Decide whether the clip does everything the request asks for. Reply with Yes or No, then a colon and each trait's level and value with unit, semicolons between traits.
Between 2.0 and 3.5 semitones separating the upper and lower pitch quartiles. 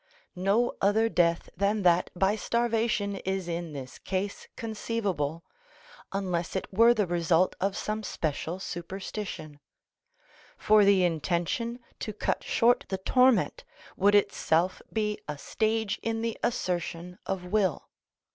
No: average, 3.9 semitones